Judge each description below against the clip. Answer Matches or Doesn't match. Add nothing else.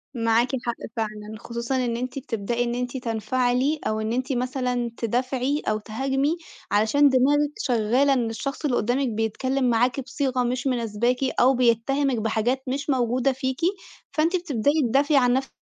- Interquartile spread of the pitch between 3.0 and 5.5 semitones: Doesn't match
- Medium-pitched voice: Doesn't match